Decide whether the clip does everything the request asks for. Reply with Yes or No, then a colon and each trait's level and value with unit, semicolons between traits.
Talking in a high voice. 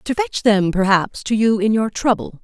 Yes: high, 215 Hz